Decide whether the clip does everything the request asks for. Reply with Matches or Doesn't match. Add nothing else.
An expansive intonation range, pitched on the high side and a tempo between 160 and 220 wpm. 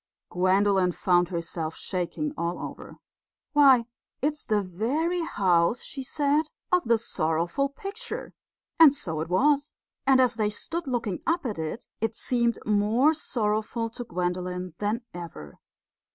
Doesn't match